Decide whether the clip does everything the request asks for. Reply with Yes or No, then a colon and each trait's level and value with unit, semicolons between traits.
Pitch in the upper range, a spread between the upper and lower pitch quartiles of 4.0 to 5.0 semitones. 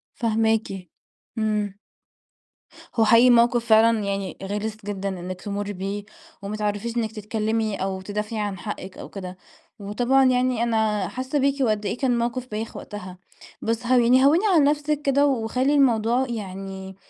No: high, 220 Hz; average, 3.2 semitones